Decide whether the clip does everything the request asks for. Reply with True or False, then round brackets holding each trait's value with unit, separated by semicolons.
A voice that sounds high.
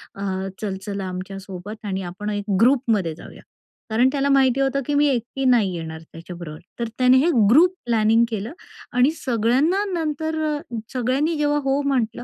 True (240 Hz)